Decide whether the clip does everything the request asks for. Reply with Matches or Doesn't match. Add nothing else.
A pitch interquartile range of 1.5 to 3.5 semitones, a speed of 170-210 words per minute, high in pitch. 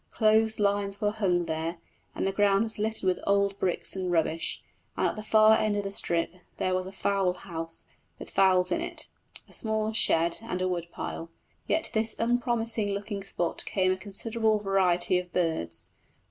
Matches